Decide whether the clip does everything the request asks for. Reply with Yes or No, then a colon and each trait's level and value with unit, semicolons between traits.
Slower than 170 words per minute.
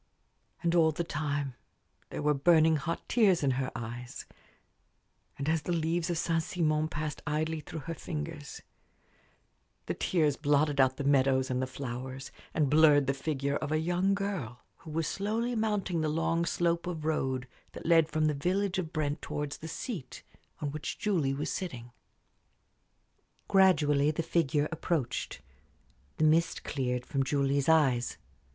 Yes: average, 160 wpm